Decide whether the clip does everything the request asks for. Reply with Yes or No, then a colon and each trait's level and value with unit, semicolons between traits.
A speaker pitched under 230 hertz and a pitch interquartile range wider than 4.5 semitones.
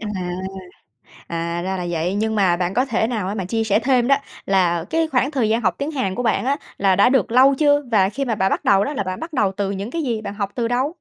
Yes: high, 220 Hz; average, 5.1 semitones